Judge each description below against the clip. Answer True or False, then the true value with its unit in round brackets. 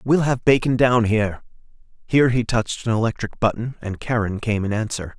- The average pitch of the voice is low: True (115 Hz)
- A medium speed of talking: True (185 wpm)